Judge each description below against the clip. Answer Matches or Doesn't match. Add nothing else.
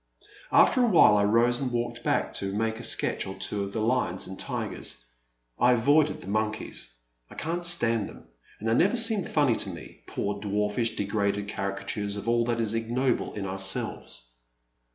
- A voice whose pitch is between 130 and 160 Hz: Doesn't match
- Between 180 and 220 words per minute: Matches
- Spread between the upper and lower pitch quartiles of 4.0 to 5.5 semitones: Doesn't match